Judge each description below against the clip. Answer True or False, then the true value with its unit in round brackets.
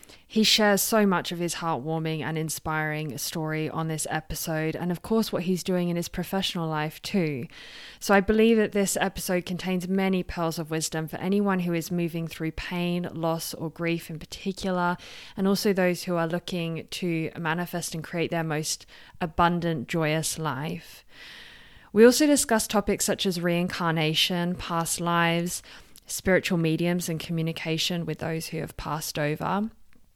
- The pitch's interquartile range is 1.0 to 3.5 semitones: True (2.4 semitones)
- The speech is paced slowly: False (160 wpm)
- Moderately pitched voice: True (170 Hz)